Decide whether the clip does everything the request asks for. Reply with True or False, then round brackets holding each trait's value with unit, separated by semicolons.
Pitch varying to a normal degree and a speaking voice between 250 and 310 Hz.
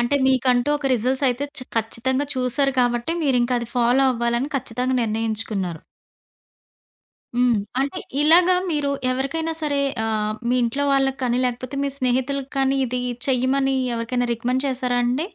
False (2.3 semitones; 255 Hz)